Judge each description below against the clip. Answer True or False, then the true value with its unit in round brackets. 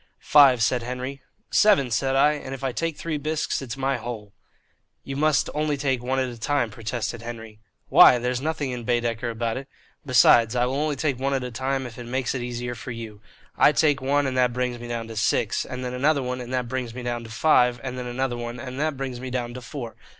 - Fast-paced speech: True (240 wpm)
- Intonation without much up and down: True (2.3 semitones)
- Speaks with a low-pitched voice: True (125 Hz)